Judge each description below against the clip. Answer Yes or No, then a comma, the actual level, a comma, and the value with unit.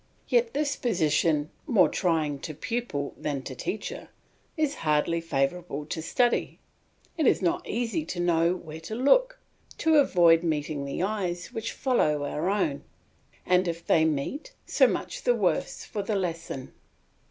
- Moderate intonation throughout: No, wide, 6.9 semitones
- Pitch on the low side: No, medium, 175 Hz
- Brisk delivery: No, average, 155 wpm